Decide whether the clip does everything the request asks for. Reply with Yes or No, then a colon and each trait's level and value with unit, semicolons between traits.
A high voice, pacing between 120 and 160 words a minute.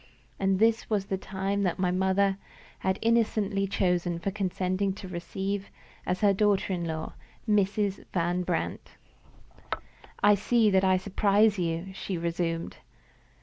Yes: high, 195 Hz; average, 140 wpm